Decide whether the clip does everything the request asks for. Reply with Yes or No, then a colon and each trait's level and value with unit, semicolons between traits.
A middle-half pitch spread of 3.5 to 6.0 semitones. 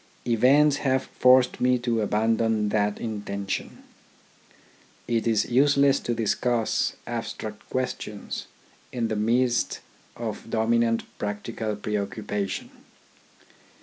No: average, 2.8 semitones